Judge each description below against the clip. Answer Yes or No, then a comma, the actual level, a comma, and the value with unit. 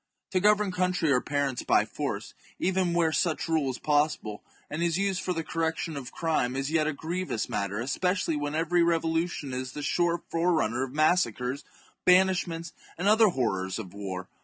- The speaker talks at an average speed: Yes, average, 185 wpm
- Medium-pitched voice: Yes, medium, 160 Hz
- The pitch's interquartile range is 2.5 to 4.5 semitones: No, average, 4.9 semitones